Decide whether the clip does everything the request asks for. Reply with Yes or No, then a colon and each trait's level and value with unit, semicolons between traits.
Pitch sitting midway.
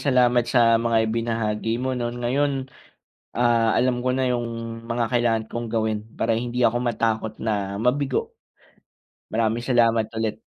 No: low, 120 Hz